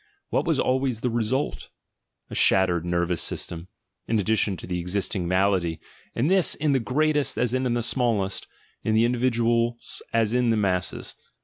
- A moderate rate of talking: Yes, average, 150 wpm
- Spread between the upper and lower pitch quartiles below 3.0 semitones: No, average, 4.8 semitones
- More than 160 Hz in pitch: No, low, 115 Hz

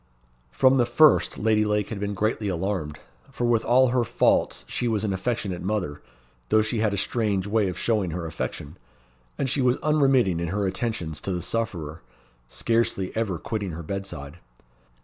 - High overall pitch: No, low, 105 Hz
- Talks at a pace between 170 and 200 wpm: Yes, average, 175 wpm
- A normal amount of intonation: Yes, average, 4.4 semitones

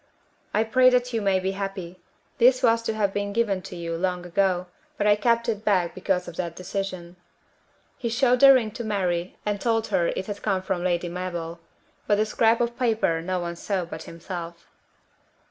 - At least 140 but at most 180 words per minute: No, average, 195 wpm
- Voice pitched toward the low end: No, high, 195 Hz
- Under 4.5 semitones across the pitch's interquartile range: Yes, average, 4.1 semitones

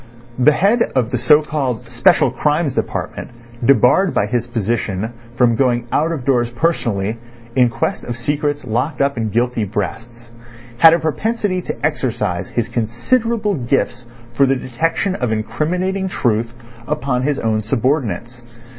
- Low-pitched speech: Yes, low, 125 Hz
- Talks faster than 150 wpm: No, average, 145 wpm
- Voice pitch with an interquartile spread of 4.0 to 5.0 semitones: Yes, average, 4.5 semitones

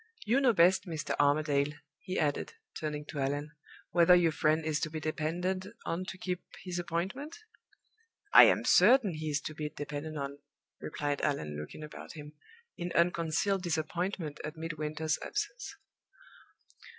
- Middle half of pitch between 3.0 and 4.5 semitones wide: Yes, average, 3.3 semitones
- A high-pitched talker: No, medium, 160 Hz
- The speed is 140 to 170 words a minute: Yes, average, 150 wpm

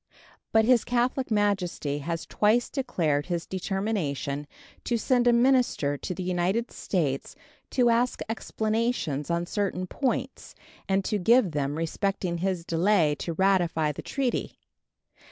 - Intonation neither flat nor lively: No, wide, 5.8 semitones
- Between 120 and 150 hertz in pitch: No, high, 190 Hz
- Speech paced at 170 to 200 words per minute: No, slow, 135 wpm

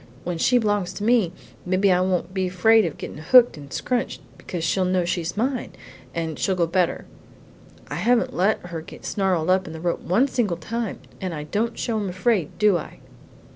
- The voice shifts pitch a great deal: No, average, 4.3 semitones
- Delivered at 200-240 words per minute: Yes, fast, 205 wpm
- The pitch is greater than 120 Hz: Yes, medium, 185 Hz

